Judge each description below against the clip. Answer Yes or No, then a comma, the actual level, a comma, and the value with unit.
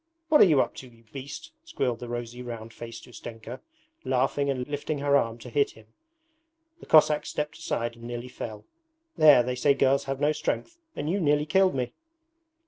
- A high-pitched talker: No, low, 130 Hz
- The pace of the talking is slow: No, average, 190 wpm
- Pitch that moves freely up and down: No, average, 3.8 semitones